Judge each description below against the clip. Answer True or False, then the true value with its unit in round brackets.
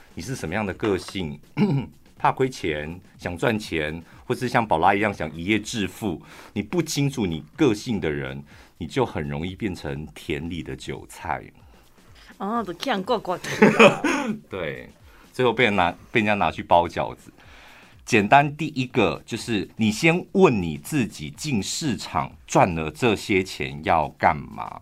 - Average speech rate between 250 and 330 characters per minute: False (215 characters per minute)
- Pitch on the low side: True (105 Hz)